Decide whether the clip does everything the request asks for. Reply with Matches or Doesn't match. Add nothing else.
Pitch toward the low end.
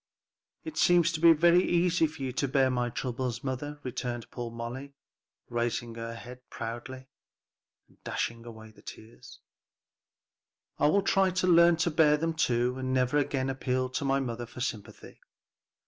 Matches